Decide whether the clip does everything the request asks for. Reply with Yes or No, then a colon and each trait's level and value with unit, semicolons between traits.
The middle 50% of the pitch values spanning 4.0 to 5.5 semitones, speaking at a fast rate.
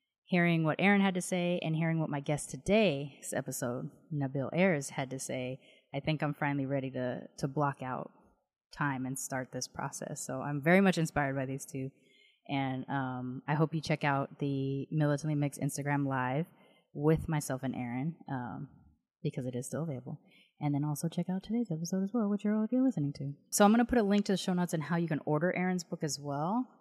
Yes: average, 4.4 semitones; fast, 215 wpm